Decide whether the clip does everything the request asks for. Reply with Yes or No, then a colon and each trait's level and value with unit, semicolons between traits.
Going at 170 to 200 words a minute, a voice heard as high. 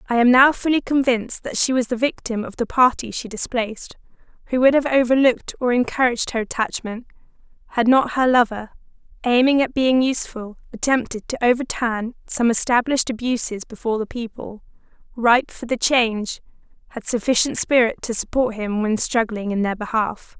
No: average, 160 wpm; high, 240 Hz